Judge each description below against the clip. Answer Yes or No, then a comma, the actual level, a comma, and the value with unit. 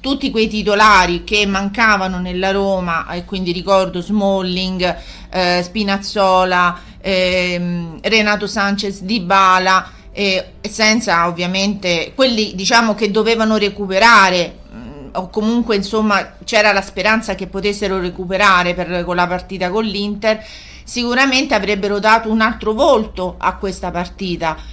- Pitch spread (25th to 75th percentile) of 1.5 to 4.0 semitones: Yes, average, 2.8 semitones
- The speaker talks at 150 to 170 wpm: No, average, 125 wpm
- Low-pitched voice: No, high, 195 Hz